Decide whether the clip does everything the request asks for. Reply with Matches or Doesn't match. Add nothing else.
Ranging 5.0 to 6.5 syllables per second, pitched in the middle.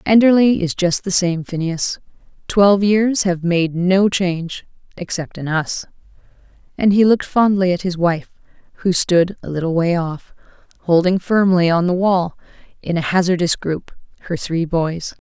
Doesn't match